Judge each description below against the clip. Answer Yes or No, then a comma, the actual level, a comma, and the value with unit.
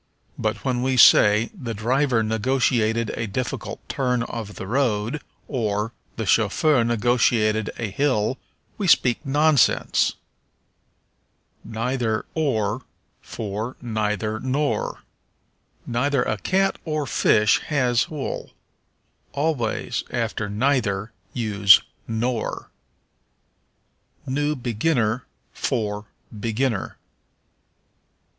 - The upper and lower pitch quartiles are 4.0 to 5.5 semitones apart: No, average, 3.6 semitones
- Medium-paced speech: No, slow, 90 wpm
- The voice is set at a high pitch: No, low, 115 Hz